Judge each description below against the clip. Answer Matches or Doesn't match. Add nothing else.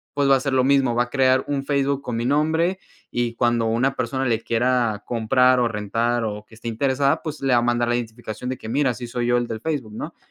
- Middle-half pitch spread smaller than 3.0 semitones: Matches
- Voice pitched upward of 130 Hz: Doesn't match